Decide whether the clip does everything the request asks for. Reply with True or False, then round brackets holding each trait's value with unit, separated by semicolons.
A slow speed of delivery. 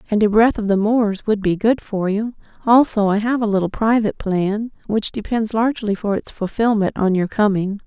False (205 wpm)